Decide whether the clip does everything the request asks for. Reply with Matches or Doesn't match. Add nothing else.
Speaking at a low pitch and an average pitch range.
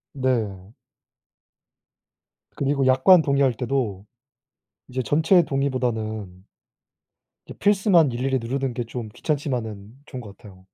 Matches